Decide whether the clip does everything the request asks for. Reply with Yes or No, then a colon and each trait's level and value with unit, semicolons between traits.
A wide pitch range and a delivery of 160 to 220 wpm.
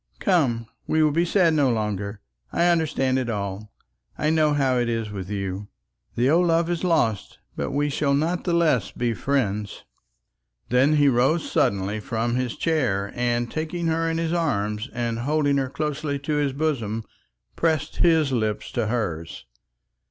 Yes: wide, 5.9 semitones; average, 165 wpm